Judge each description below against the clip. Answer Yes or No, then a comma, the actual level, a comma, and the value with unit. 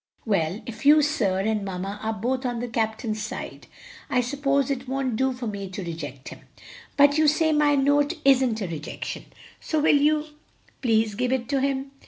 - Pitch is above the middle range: Yes, very high, 250 Hz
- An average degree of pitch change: Yes, average, 4.8 semitones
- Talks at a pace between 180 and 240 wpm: Yes, average, 190 wpm